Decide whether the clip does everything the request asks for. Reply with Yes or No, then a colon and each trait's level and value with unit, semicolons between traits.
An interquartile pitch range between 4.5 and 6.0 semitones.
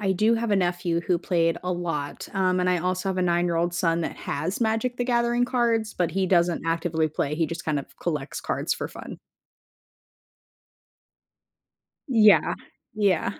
No: average, 4.0 semitones